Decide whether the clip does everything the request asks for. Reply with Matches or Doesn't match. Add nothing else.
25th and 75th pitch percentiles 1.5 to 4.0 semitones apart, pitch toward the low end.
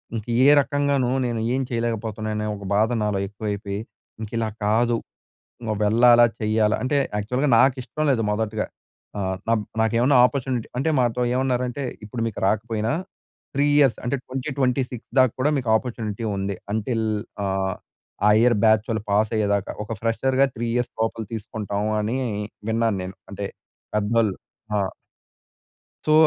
Matches